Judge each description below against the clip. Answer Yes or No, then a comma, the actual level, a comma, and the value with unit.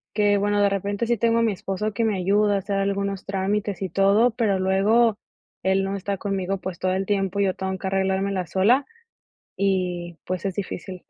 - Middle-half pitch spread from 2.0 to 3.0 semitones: No, narrow, 1.4 semitones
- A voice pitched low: No, high, 195 Hz